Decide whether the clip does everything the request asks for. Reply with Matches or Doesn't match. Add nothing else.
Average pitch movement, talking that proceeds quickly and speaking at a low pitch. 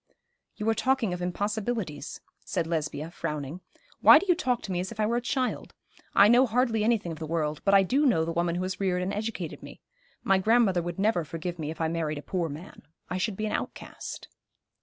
Doesn't match